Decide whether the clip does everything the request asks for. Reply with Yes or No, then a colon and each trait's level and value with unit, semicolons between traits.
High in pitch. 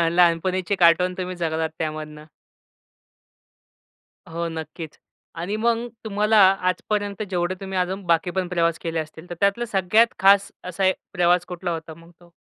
No: medium, 180 Hz